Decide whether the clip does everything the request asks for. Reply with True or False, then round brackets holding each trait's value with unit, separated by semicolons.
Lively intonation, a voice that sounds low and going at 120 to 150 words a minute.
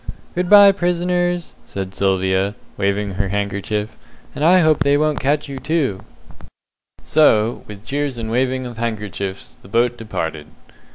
True (7.2 semitones; 120 Hz; 145 wpm)